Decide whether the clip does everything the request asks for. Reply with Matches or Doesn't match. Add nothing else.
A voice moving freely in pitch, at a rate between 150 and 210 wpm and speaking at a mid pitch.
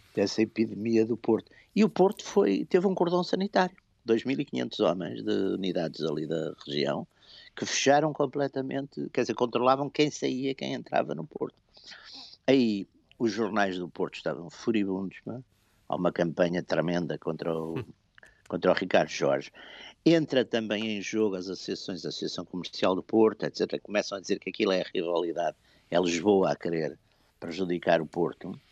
Doesn't match